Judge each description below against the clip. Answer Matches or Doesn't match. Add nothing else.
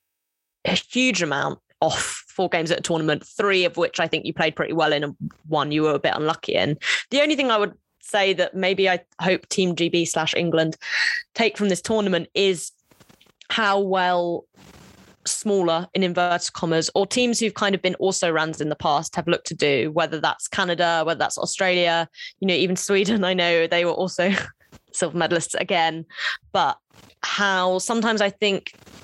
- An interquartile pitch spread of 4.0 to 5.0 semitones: Doesn't match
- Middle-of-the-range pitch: Matches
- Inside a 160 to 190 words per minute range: Matches